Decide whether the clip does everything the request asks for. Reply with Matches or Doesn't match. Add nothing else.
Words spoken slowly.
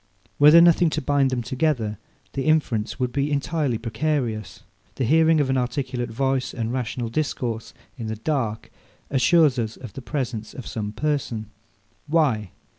Doesn't match